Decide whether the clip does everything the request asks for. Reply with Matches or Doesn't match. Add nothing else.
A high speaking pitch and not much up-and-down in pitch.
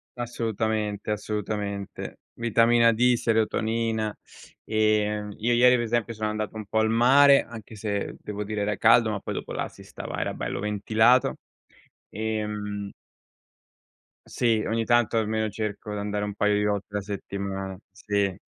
Doesn't match